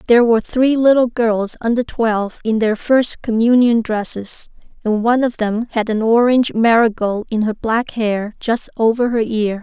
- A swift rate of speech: No, average, 175 wpm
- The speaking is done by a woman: Yes, female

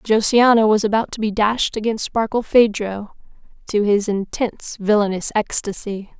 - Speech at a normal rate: No, slow, 125 wpm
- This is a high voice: Yes, high, 215 Hz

